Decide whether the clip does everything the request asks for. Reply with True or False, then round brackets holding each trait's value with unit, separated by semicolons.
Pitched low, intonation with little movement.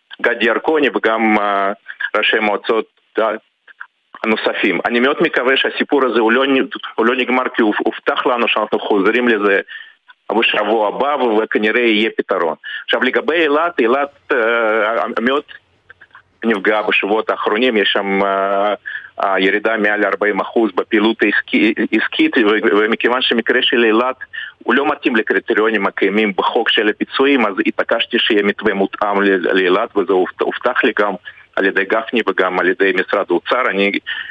False (110 Hz; 5.2 semitones)